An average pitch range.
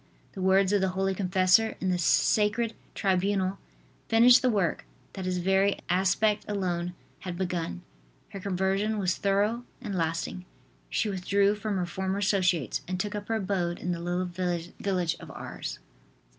No: narrow, 2.1 semitones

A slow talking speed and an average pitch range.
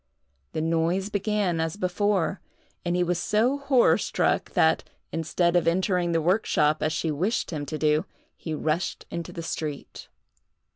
No: average, 155 wpm; average, 3.2 semitones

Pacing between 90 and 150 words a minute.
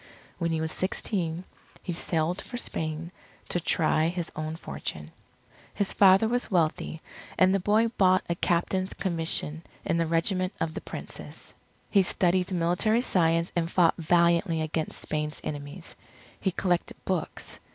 Yes: average, 145 wpm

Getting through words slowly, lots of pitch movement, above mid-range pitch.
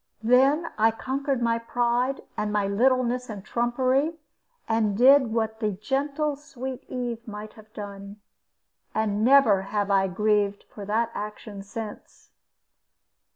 No: slow, 130 wpm; average, 3.7 semitones; high, 225 Hz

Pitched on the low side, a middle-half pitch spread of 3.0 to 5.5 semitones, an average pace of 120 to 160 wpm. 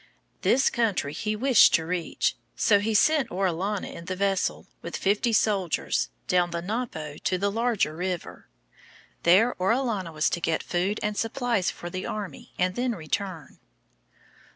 No: high, 195 Hz; average, 4.1 semitones; average, 150 wpm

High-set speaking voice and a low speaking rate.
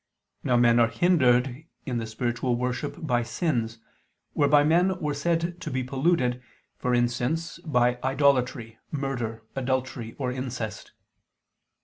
No: low, 125 Hz; slow, 125 wpm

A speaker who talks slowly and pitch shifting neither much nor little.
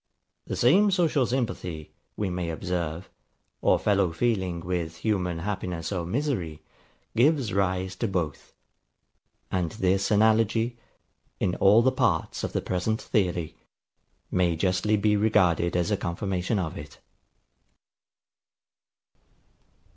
Yes: slow, 115 wpm; average, 3.9 semitones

